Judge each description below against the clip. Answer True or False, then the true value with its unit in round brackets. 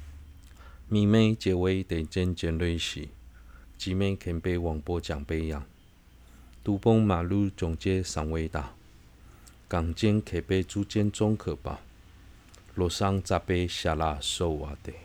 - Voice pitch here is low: True (85 Hz)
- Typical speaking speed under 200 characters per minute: True (185 characters per minute)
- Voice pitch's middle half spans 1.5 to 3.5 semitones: True (3.2 semitones)